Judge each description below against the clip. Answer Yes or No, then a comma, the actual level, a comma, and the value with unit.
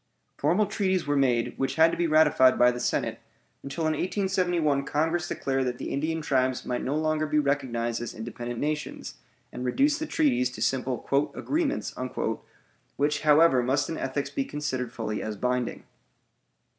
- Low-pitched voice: No, medium, 145 Hz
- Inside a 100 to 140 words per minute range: No, average, 165 wpm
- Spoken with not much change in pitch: No, average, 4.2 semitones